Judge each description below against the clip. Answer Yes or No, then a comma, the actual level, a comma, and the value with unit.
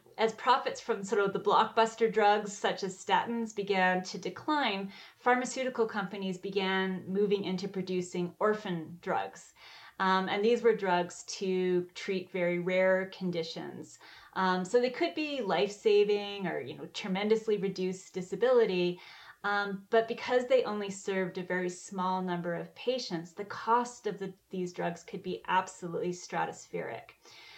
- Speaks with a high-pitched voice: Yes, high, 195 Hz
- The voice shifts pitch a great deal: No, average, 3.2 semitones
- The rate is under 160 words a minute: Yes, average, 145 wpm